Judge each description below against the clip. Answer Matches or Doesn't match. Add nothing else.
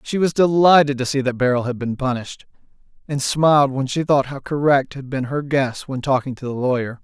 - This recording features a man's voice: Matches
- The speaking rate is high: Matches